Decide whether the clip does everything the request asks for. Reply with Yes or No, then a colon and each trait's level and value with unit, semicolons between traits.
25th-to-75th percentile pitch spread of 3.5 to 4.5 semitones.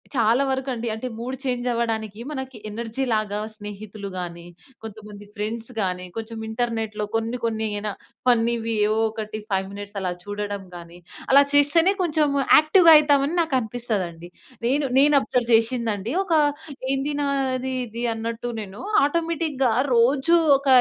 Yes: average, 4.1 semitones